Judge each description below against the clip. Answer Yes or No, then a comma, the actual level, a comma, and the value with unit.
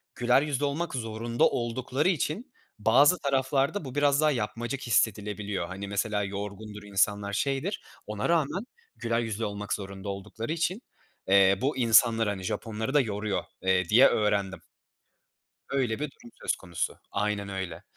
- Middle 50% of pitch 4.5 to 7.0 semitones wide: Yes, average, 5.2 semitones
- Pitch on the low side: Yes, low, 110 Hz